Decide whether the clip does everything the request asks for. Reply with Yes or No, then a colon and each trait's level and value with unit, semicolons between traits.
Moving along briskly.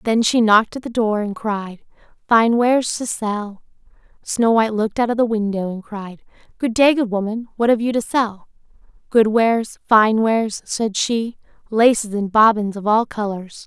No: average, 185 wpm